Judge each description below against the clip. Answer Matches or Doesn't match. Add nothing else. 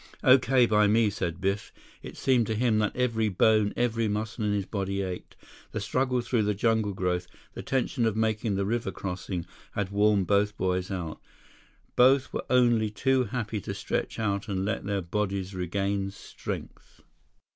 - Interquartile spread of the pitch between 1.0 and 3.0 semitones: Matches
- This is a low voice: Matches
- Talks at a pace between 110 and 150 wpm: Doesn't match